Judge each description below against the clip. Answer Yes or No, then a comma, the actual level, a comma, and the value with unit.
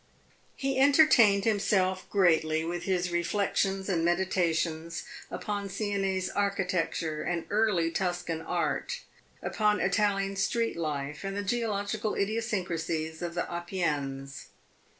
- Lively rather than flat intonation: No, average, 3.4 semitones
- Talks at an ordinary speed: No, slow, 110 wpm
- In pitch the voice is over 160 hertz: Yes, medium, 185 Hz